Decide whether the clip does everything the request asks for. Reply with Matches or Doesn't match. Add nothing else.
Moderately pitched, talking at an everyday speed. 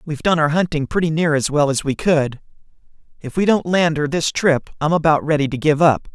Doesn't match